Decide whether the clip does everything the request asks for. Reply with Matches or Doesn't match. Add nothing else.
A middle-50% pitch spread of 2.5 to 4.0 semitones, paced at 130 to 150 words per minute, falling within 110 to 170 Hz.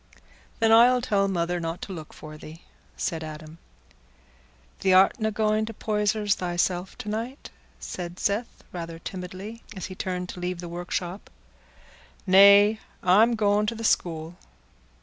Doesn't match